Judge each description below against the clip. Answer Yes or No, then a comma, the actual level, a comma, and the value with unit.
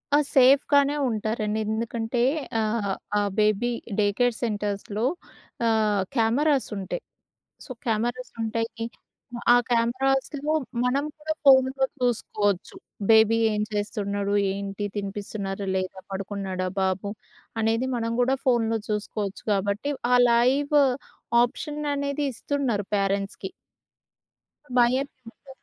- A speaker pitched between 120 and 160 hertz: No, high, 225 Hz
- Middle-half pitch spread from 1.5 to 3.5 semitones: No, average, 4.0 semitones